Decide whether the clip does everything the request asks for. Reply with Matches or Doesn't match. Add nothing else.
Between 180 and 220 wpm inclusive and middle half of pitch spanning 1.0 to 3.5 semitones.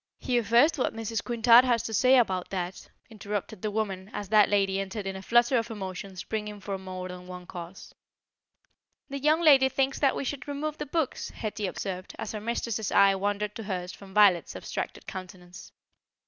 Doesn't match